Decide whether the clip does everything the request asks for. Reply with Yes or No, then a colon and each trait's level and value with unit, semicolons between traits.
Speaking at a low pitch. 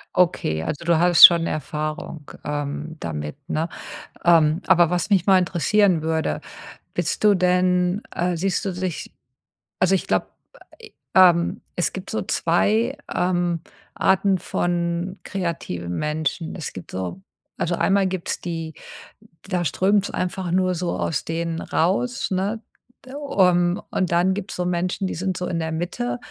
No: medium, 175 Hz